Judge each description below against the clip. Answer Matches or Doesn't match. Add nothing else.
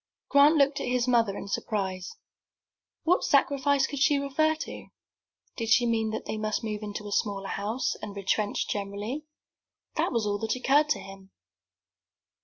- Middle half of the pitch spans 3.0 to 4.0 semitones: Doesn't match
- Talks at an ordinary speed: Matches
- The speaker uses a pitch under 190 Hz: Doesn't match